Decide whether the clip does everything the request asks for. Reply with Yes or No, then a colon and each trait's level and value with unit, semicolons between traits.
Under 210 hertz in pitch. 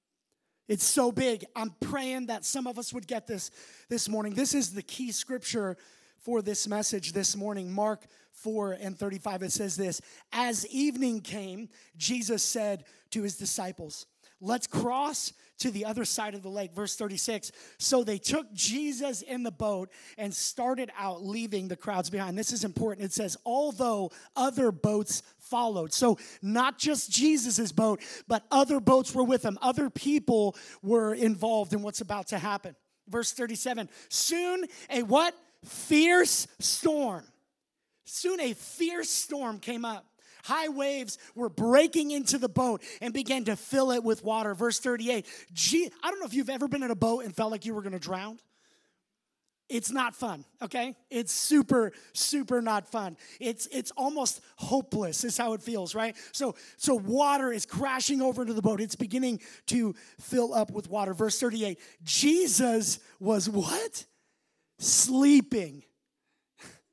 No: high, 230 Hz